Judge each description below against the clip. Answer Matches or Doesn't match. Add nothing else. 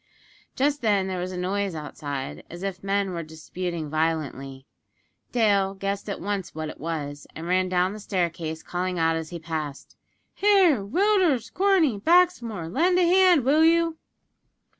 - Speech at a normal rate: Matches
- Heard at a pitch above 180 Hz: Matches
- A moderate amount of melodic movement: Doesn't match